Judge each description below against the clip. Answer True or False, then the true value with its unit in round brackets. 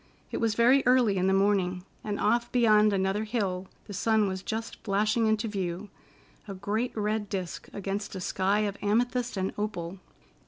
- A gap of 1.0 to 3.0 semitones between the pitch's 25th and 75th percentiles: True (2.4 semitones)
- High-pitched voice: True (205 Hz)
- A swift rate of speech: False (165 wpm)